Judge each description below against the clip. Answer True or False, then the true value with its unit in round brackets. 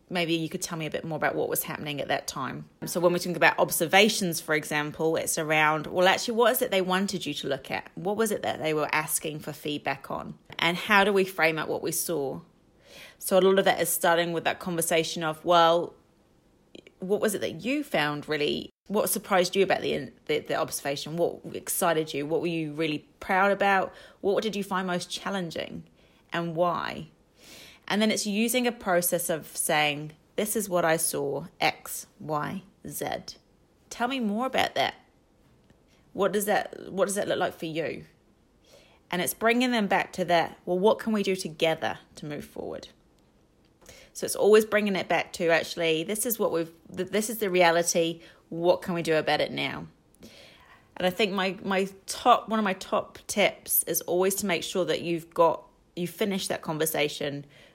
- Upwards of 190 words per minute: True (200 wpm)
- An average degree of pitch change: True (3.4 semitones)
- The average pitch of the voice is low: False (175 Hz)